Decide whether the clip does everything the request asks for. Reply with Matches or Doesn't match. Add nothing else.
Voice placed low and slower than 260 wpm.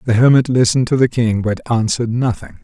Matches